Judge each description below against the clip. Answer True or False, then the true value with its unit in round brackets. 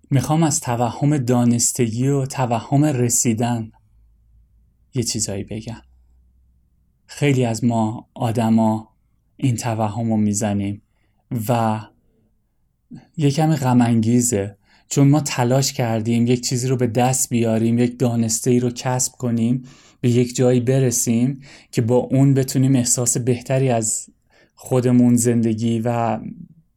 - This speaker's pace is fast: False (120 wpm)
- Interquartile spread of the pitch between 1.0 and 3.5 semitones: True (2.4 semitones)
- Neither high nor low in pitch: False (120 Hz)